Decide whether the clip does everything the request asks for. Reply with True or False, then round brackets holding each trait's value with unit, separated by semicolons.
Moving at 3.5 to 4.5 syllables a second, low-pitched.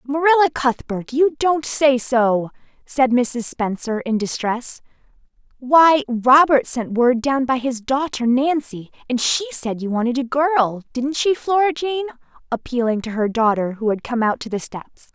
False (4.2 syllables/s; 260 Hz)